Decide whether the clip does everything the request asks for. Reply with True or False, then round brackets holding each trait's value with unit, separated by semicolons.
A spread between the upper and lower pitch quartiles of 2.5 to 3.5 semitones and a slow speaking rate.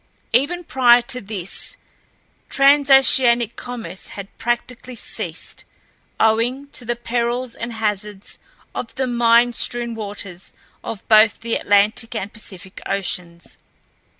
True (3.0 semitones; 115 wpm)